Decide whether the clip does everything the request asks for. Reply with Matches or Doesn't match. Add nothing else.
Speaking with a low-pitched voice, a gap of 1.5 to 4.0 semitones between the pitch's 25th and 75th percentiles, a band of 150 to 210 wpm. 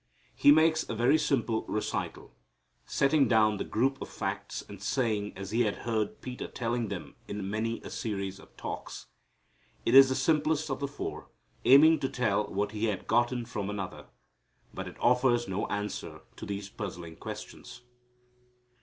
Doesn't match